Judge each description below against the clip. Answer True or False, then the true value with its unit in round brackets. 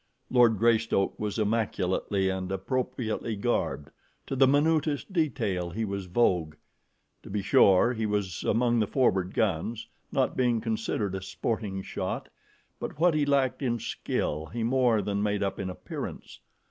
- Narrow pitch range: False (4.2 semitones)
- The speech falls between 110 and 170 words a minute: True (150 wpm)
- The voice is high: False (110 Hz)